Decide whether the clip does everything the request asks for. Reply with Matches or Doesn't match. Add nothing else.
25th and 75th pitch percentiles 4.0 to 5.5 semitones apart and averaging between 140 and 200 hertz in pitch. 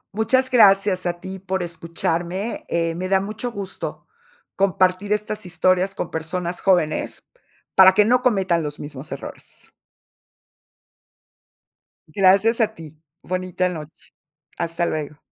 Doesn't match